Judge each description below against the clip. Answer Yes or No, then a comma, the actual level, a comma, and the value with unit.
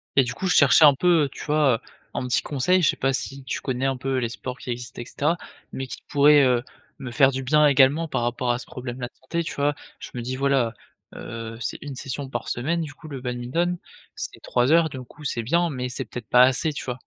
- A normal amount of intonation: Yes, average, 3.1 semitones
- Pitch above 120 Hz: Yes, low, 135 Hz